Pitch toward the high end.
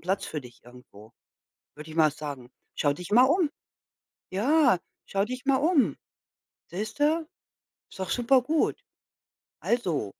Yes: high, 195 Hz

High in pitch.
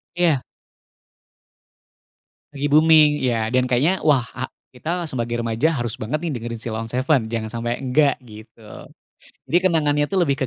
No: low, 130 Hz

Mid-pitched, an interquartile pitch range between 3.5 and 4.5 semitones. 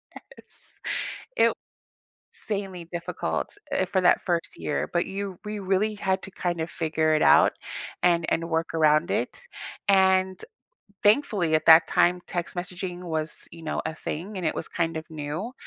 No: medium, 175 Hz; average, 2.8 semitones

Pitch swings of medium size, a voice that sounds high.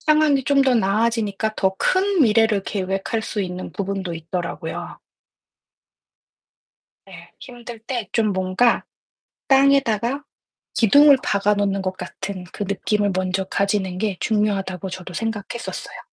Yes: average, 3.6 semitones; high, 205 Hz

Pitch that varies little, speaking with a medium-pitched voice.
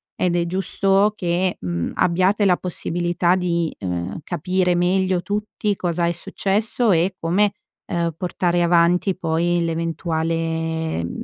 Yes: narrow, 2.2 semitones; medium, 175 Hz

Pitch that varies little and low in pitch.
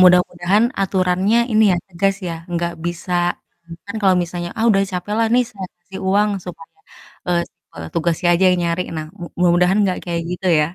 No: narrow, 2.2 semitones; medium, 180 Hz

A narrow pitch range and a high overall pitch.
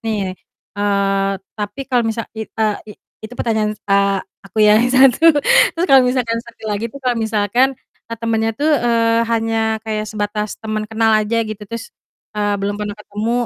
Yes: narrow, 1.8 semitones; high, 220 Hz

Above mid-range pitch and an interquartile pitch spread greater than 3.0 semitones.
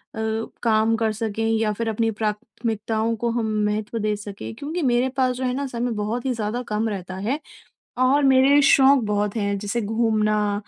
No: high, 225 Hz; average, 2.7 semitones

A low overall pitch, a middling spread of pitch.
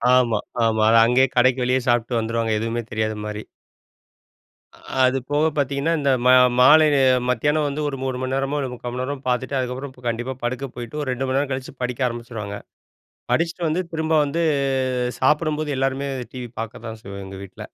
Yes: low, 130 Hz; average, 3.1 semitones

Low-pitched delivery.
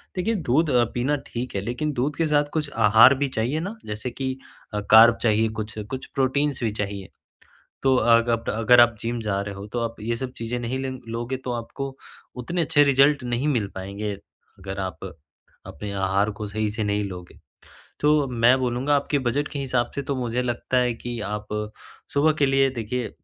Yes: low, 120 Hz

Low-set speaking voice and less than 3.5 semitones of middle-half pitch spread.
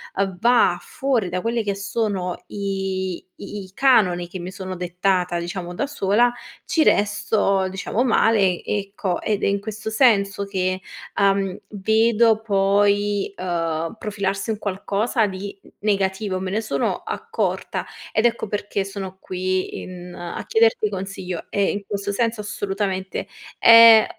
No: high, 200 Hz; narrow, 2.6 semitones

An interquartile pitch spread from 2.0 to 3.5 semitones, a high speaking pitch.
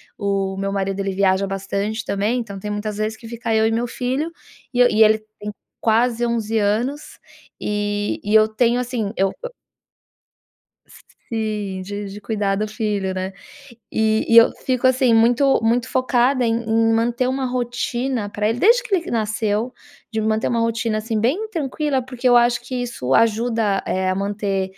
Yes: average, 3.0 semitones; high, 225 Hz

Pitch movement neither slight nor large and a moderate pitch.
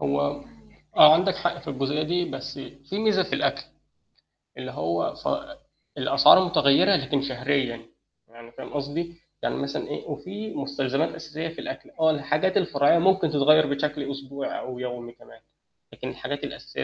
Yes: average, 3.6 semitones; medium, 145 Hz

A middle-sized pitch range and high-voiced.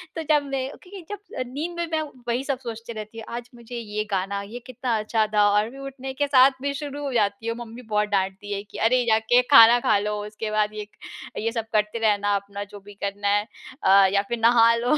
Yes: average, 3.5 semitones; high, 225 Hz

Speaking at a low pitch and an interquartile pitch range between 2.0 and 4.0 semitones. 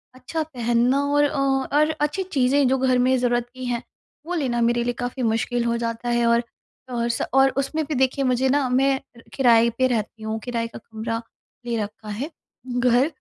No: very high, 250 Hz; narrow, 2.4 semitones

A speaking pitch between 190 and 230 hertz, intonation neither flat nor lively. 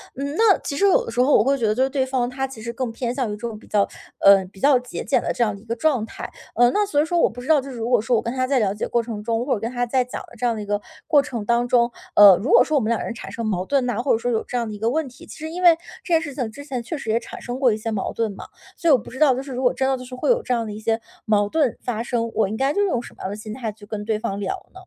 No: high, 240 Hz; average, 3.5 semitones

